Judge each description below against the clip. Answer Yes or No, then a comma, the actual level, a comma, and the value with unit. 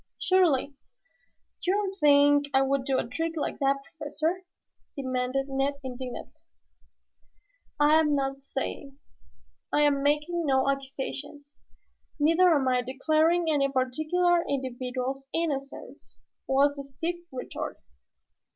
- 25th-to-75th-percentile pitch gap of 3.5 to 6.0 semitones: No, average, 2.7 semitones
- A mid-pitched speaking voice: No, very high, 280 Hz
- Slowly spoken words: Yes, slow, 115 wpm